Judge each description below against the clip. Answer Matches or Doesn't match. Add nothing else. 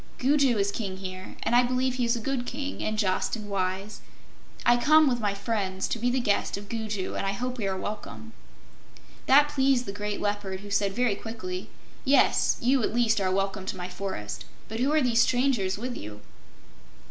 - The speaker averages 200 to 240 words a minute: Matches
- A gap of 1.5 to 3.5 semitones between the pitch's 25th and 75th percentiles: Doesn't match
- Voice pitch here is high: Matches